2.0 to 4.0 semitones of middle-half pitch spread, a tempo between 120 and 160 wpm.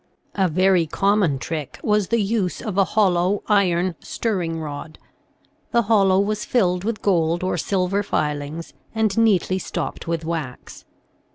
Yes: average, 3.7 semitones; average, 145 wpm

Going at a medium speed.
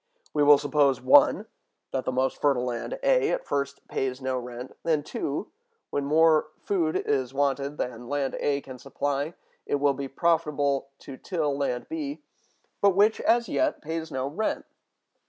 Yes: average, 165 wpm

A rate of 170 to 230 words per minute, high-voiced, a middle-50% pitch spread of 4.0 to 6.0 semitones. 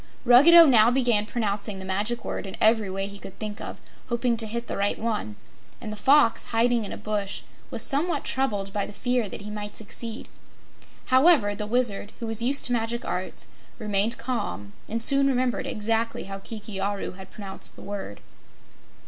No: average, 185 wpm; high, 220 Hz; average, 3.1 semitones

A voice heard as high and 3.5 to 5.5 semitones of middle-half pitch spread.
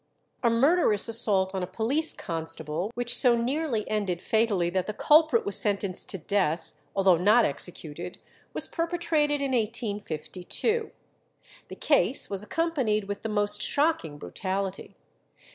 Yes: high, 210 Hz; average, 5.0 semitones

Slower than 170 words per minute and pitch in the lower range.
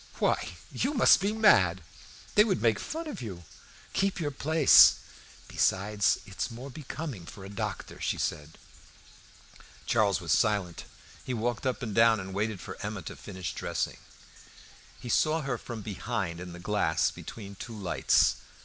Yes: average, 160 wpm; low, 110 Hz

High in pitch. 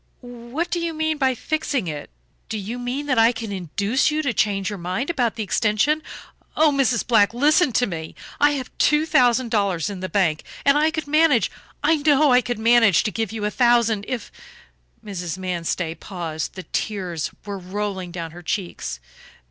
Yes: high, 225 Hz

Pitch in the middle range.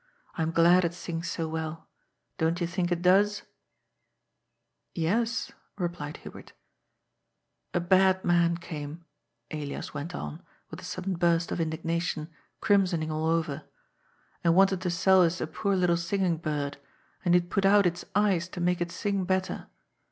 Yes: medium, 175 Hz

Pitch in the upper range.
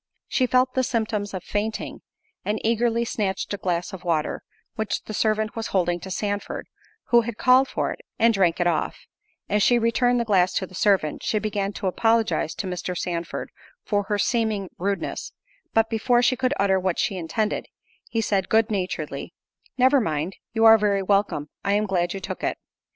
Yes: high, 205 Hz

